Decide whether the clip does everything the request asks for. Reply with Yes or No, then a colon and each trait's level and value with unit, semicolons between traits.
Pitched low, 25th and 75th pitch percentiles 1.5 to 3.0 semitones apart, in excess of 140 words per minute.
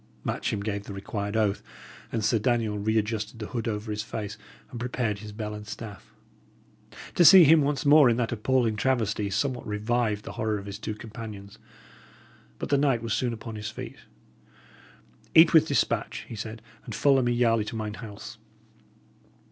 Yes: low, 110 Hz; narrow, 2.5 semitones; average, 180 wpm